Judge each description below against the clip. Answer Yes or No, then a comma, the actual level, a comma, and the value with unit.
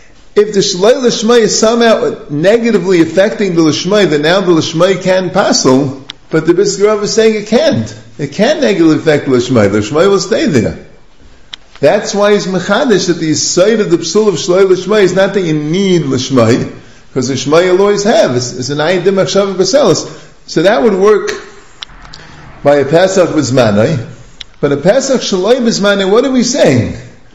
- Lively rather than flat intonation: Yes, wide, 6.3 semitones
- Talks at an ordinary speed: Yes, average, 170 wpm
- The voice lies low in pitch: No, medium, 185 Hz